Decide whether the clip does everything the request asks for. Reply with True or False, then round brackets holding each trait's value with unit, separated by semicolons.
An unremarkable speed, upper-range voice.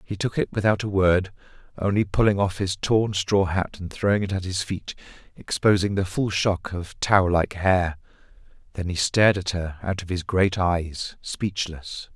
False (190 wpm; 95 Hz)